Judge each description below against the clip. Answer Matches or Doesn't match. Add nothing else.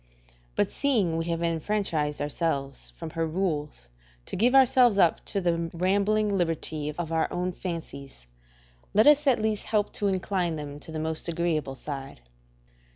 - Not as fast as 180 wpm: Matches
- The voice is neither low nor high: Matches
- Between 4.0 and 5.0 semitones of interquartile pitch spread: Matches